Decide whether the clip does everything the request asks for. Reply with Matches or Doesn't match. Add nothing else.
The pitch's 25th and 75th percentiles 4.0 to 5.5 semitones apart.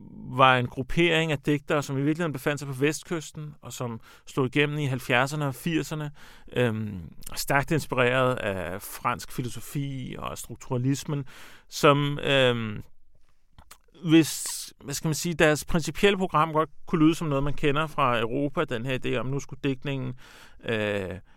Doesn't match